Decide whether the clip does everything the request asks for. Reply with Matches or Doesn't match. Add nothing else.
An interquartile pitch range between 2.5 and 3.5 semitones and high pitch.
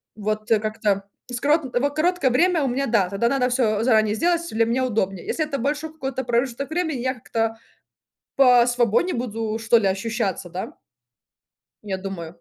Doesn't match